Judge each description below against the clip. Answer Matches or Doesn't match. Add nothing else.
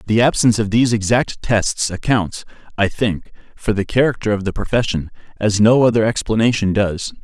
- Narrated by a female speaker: Doesn't match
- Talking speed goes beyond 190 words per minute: Doesn't match